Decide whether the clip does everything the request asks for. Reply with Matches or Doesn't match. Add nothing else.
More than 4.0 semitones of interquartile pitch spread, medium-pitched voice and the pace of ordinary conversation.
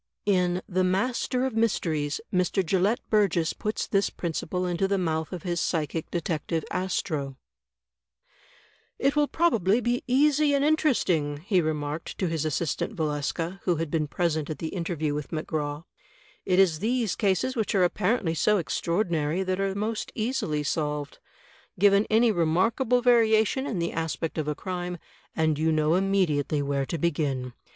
Matches